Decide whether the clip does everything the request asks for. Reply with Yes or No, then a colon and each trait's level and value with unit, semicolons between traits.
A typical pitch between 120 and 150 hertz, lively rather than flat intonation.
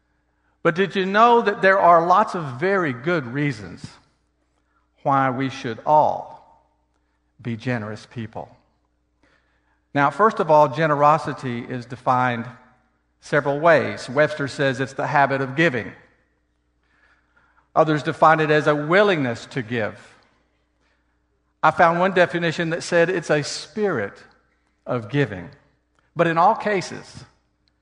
Yes: medium, 140 Hz; wide, 6.5 semitones